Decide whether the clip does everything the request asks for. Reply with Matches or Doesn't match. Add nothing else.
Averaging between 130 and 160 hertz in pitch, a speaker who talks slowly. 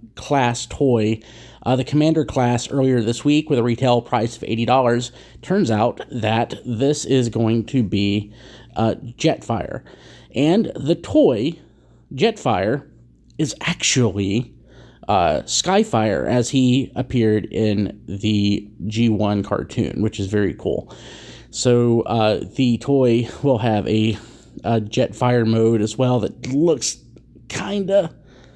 Doesn't match